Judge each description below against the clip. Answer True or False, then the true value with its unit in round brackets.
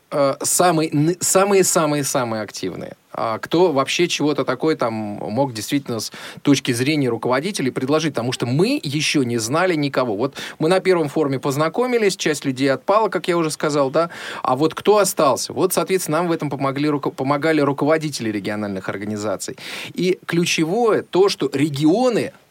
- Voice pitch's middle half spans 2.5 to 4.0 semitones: False (4.4 semitones)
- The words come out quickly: False (150 wpm)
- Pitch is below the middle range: False (150 Hz)